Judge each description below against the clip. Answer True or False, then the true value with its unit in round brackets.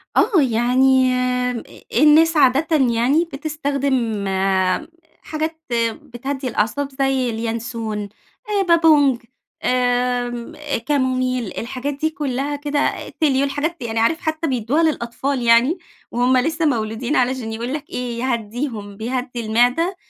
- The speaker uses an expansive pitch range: False (3.7 semitones)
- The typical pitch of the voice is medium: False (260 Hz)